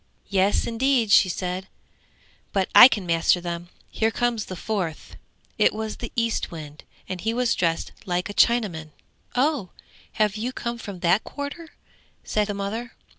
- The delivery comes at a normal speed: Yes, average, 155 wpm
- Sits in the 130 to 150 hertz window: No, high, 205 Hz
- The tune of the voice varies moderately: Yes, average, 4.6 semitones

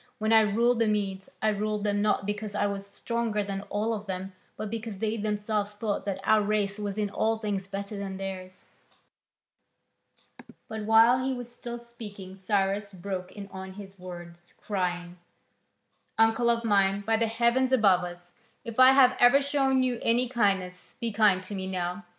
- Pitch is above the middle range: Yes, high, 210 Hz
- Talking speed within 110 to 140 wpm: No, average, 180 wpm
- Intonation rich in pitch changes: No, average, 2.7 semitones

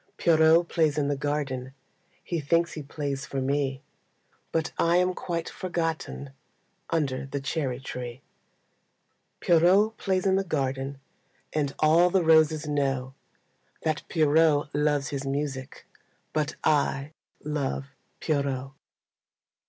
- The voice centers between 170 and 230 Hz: No, medium, 150 Hz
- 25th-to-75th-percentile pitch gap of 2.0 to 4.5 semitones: Yes, average, 3.0 semitones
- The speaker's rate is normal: No, slow, 120 wpm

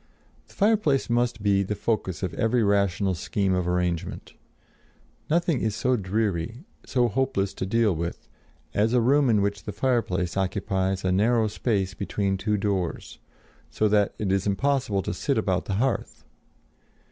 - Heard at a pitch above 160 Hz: No, low, 105 Hz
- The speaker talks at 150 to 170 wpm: Yes, average, 160 wpm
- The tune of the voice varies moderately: Yes, average, 3.7 semitones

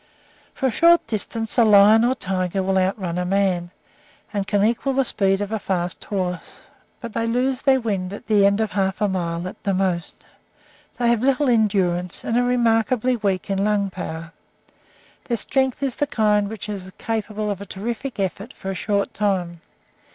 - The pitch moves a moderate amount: Yes, average, 3.3 semitones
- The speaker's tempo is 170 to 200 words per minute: Yes, average, 190 wpm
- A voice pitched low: No, high, 205 Hz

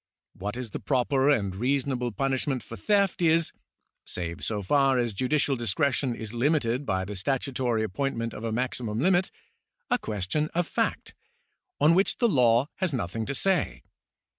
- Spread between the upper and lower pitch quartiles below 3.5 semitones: No, average, 4.6 semitones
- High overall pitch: No, low, 125 Hz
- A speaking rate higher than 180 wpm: No, average, 160 wpm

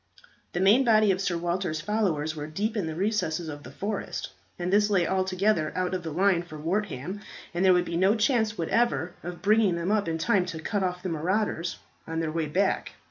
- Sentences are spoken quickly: Yes, fast, 215 wpm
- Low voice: No, medium, 185 Hz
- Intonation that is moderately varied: Yes, average, 3.8 semitones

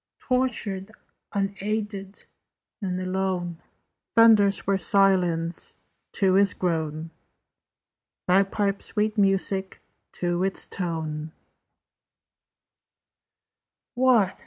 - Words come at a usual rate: No, slow, 70 wpm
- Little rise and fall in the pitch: Yes, narrow, 2.3 semitones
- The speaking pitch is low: No, high, 195 Hz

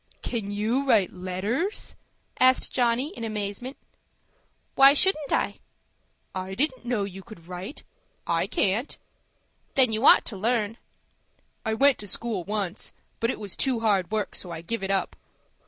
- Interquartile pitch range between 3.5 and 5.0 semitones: Yes, average, 4.4 semitones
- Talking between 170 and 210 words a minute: No, average, 155 wpm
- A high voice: Yes, high, 220 Hz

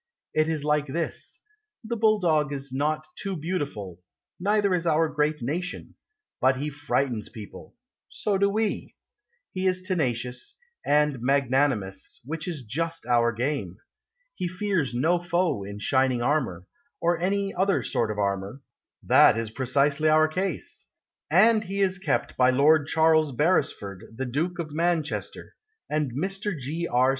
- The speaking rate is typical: Yes, average, 145 wpm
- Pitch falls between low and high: Yes, medium, 150 Hz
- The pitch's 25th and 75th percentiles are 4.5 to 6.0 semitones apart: Yes, wide, 5.6 semitones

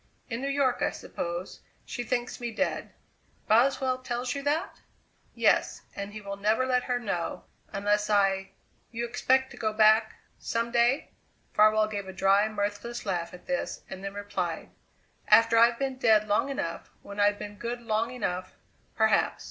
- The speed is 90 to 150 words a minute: No, average, 170 wpm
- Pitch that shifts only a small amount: No, average, 3.2 semitones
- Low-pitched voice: No, high, 220 Hz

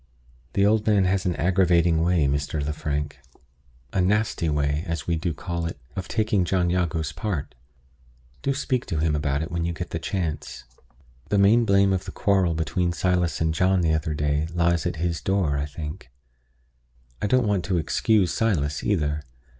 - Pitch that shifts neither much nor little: Yes, average, 3.8 semitones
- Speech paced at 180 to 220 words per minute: Yes, average, 185 wpm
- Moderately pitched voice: No, very low, 85 Hz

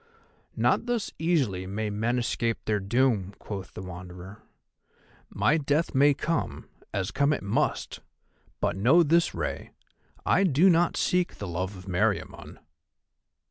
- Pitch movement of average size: No, wide, 8.3 semitones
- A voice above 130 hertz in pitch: No, low, 115 Hz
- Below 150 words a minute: Yes, average, 140 wpm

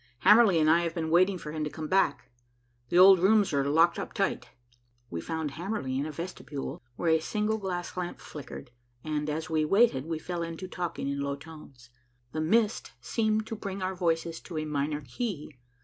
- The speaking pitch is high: No, medium, 165 Hz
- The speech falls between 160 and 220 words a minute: Yes, average, 195 wpm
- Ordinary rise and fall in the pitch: Yes, average, 3.7 semitones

